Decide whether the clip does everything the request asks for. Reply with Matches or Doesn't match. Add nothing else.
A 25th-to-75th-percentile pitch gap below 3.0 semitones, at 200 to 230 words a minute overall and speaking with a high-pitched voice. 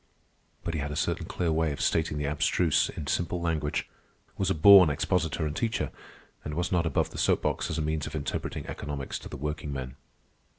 Doesn't match